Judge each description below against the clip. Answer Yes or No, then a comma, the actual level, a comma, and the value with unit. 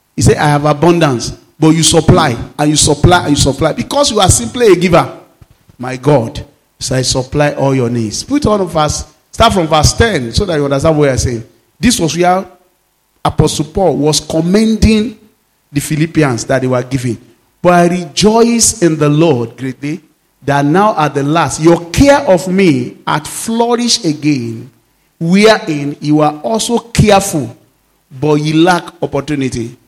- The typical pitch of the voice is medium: Yes, medium, 150 Hz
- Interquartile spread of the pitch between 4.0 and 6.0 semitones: Yes, average, 5.3 semitones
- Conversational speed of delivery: Yes, average, 170 wpm